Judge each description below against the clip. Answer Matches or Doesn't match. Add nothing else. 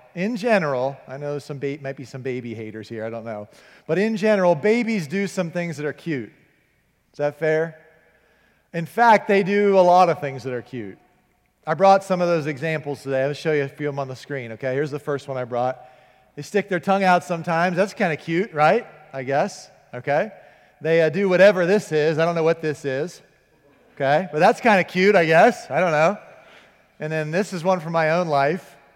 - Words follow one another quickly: Matches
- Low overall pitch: Doesn't match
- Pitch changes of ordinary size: Matches